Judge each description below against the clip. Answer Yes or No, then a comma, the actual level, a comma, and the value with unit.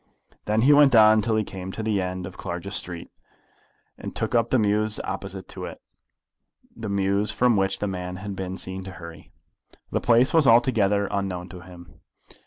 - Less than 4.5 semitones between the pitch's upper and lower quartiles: Yes, average, 2.9 semitones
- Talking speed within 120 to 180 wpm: No, average, 190 wpm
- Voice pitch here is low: Yes, low, 100 Hz